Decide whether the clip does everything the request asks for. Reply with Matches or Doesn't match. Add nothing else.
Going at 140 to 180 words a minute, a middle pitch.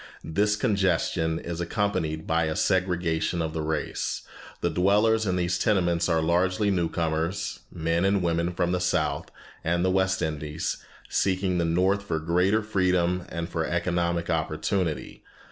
Doesn't match